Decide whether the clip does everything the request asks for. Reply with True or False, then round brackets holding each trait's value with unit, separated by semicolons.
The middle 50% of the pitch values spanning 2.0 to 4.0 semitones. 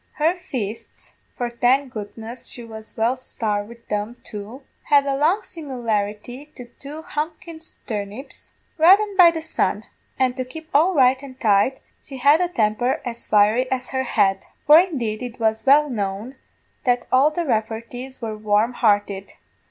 False (4.7 semitones)